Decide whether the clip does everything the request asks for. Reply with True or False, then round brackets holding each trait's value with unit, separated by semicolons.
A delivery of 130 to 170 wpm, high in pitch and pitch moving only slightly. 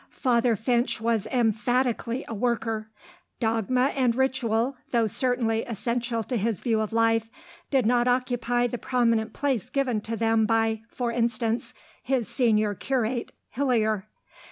True (135 wpm; 235 Hz; 1.9 semitones)